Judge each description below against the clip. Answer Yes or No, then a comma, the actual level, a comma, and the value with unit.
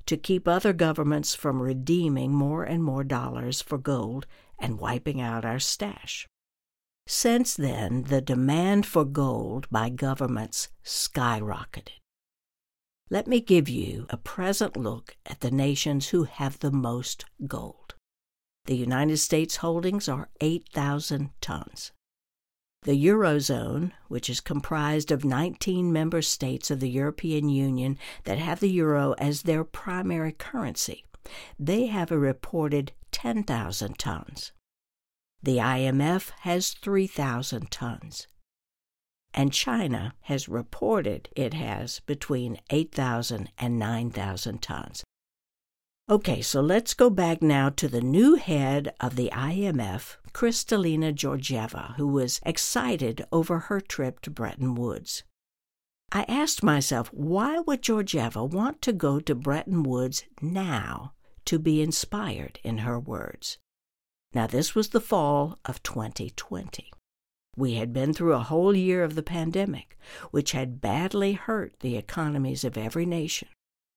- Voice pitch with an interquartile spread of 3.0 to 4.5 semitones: No, average, 5.0 semitones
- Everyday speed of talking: No, slow, 130 wpm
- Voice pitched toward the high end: No, medium, 145 Hz